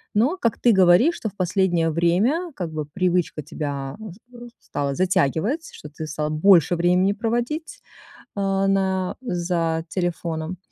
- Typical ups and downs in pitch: Yes, average, 3.8 semitones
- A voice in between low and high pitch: Yes, medium, 180 Hz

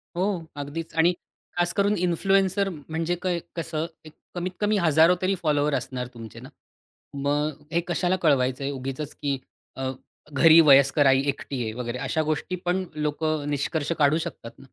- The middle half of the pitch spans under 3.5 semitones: No, average, 3.8 semitones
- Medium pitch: Yes, medium, 155 Hz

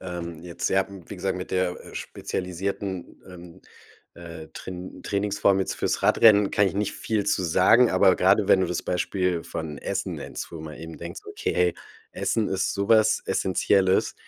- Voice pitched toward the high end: No, very low, 95 Hz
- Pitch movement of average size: No, narrow, 2.1 semitones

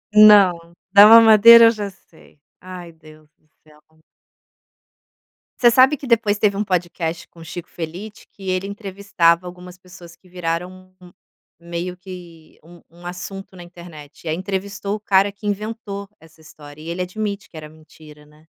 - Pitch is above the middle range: No, medium, 180 Hz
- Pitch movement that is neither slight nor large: Yes, average, 3.3 semitones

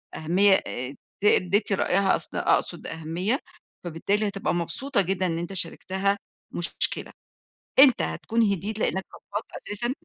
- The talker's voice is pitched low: No, high, 195 Hz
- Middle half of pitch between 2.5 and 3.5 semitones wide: Yes, average, 3.1 semitones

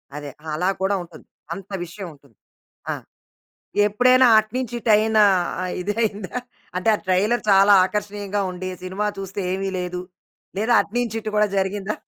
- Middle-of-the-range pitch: No, high, 200 Hz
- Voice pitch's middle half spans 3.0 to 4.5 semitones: No, narrow, 2.5 semitones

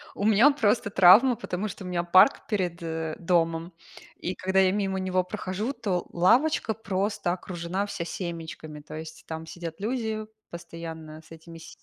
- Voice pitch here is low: No, medium, 185 Hz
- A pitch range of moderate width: Yes, average, 3.6 semitones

